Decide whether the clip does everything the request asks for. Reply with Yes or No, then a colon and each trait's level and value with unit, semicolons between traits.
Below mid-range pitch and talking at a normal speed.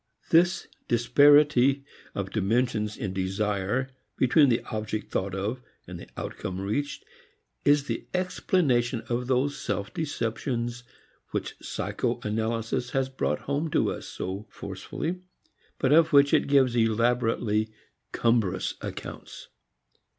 No: low, 120 Hz; slow, 120 wpm